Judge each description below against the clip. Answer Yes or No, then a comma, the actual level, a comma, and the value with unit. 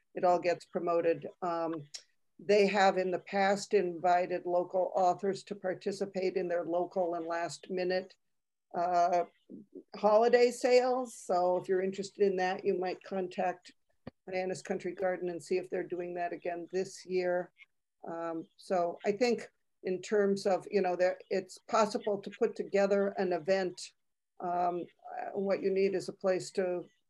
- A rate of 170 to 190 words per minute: No, average, 155 wpm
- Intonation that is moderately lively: No, narrow, 2.0 semitones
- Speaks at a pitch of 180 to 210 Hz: Yes, medium, 185 Hz